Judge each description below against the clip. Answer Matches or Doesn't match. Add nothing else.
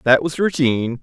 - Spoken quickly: Doesn't match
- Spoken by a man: Matches